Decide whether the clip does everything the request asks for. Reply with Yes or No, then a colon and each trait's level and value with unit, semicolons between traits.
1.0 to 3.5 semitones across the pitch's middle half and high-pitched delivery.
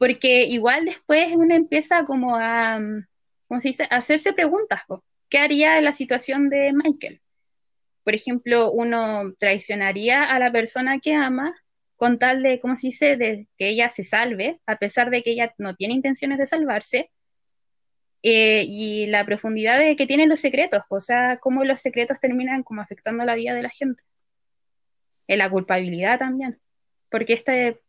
No: average, 4.0 semitones; very high, 250 Hz